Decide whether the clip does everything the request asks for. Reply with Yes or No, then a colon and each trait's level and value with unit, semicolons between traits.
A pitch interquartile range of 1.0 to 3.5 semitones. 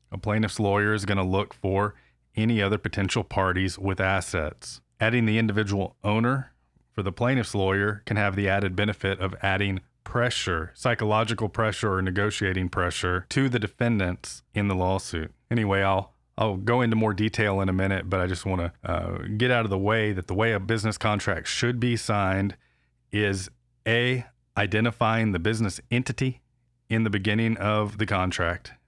Yes: average, 2.8 semitones